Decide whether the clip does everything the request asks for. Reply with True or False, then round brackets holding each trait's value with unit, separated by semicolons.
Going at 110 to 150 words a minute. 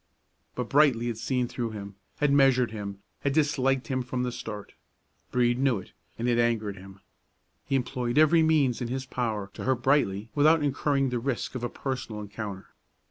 False (185 wpm)